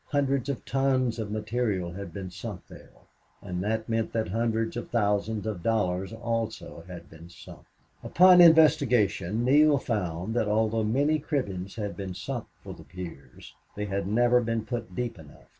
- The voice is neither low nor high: No, low, 110 Hz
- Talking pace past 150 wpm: Yes, average, 165 wpm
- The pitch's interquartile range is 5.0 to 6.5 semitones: No, average, 4.2 semitones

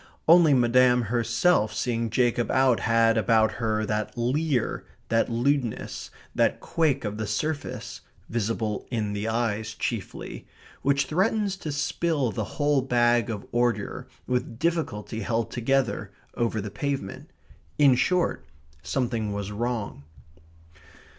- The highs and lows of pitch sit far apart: No, average, 3.8 semitones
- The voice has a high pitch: No, low, 120 Hz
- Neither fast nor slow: No, slow, 125 wpm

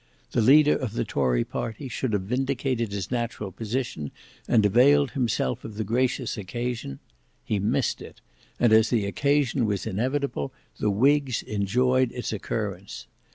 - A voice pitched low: Yes, low, 115 Hz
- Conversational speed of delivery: Yes, average, 150 wpm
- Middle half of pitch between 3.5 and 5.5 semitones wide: Yes, average, 4.1 semitones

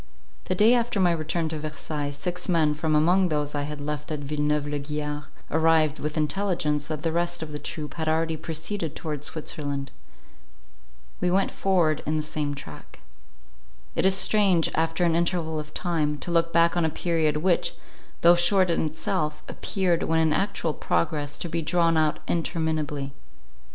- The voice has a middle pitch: Yes, medium, 160 Hz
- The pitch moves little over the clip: Yes, narrow, 2.3 semitones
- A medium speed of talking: Yes, average, 175 wpm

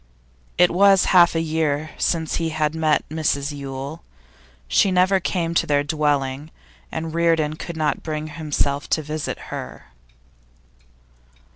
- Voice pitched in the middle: Yes, medium, 155 Hz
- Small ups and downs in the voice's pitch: Yes, narrow, 2.1 semitones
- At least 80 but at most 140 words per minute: Yes, slow, 135 wpm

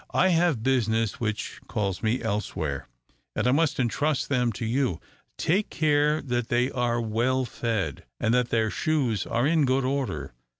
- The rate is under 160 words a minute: No, average, 165 wpm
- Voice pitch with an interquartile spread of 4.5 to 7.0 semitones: No, average, 4.0 semitones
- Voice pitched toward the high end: No, low, 125 Hz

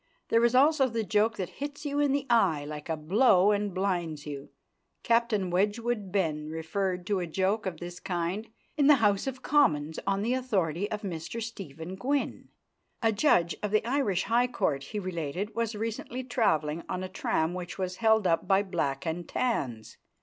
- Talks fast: No, average, 185 wpm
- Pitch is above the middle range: Yes, high, 195 Hz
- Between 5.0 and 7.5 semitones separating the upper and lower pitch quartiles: Yes, average, 5.3 semitones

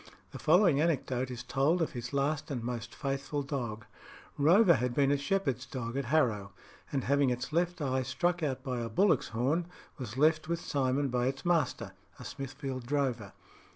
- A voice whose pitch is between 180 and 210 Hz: No, low, 135 Hz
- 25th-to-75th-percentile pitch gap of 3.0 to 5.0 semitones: Yes, average, 3.8 semitones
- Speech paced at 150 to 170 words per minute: No, average, 180 wpm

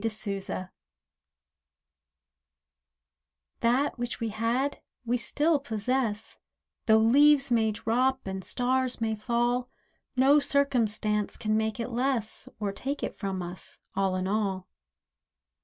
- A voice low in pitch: No, high, 230 Hz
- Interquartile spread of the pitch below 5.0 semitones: Yes, average, 3.6 semitones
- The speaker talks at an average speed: No, slow, 115 wpm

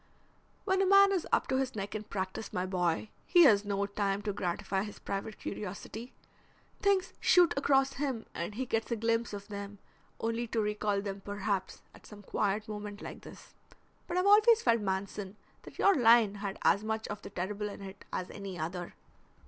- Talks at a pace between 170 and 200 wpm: Yes, average, 190 wpm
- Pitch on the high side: Yes, high, 210 Hz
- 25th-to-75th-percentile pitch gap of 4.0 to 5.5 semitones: No, average, 3.1 semitones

